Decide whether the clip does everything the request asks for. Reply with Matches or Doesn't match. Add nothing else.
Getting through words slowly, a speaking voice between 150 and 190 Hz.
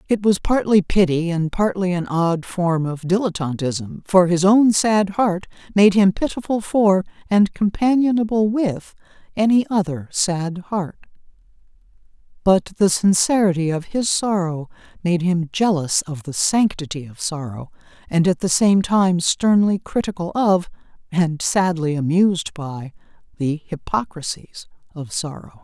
Matches